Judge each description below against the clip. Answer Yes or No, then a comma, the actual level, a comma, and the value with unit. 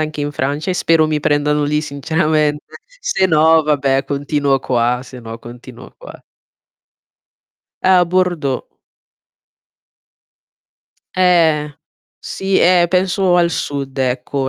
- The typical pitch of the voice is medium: Yes, medium, 150 Hz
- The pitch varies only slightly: No, average, 3.7 semitones